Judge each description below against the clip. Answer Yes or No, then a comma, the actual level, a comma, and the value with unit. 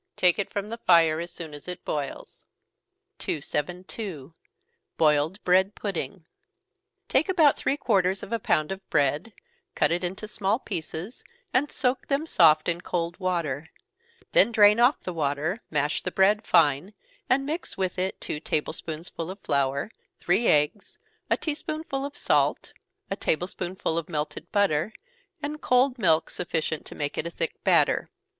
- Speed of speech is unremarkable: Yes, average, 160 wpm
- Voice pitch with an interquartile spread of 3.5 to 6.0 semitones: Yes, wide, 5.6 semitones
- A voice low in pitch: No, medium, 180 Hz